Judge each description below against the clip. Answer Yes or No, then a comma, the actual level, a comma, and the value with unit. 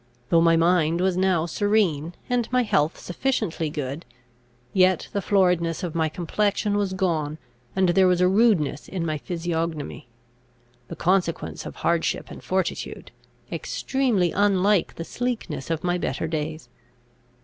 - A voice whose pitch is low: No, medium, 175 Hz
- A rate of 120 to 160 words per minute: Yes, average, 140 wpm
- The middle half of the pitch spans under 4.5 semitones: Yes, average, 3.2 semitones